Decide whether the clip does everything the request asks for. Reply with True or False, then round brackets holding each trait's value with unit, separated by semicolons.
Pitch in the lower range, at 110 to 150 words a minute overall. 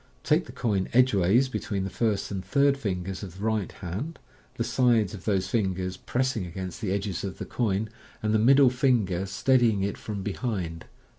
False (105 Hz; 190 wpm)